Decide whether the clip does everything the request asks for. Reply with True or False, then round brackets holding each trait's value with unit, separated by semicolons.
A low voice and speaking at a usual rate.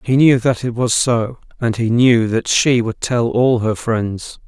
False (120 Hz; 215 wpm)